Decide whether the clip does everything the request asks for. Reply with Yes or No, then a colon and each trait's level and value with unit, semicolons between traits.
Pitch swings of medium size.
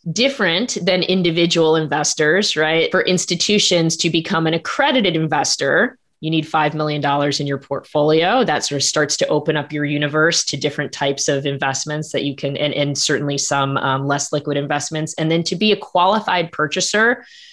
Yes: average, 3.3 semitones